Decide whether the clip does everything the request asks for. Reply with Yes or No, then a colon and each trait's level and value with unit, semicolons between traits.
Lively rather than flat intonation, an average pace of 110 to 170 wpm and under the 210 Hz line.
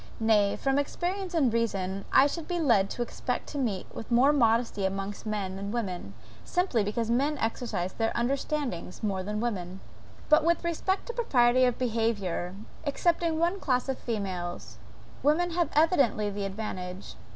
No: wide, 6.6 semitones; average, 160 wpm; high, 235 Hz